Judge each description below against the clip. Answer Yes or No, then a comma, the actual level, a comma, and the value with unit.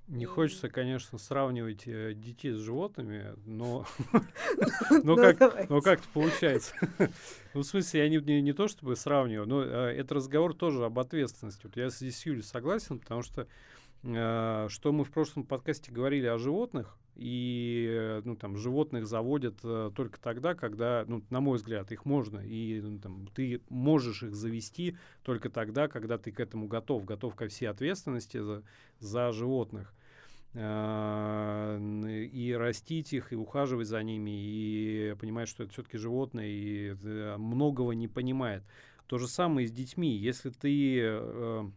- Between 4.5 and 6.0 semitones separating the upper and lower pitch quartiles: No, average, 4.0 semitones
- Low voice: Yes, low, 120 Hz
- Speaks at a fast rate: No, average, 140 wpm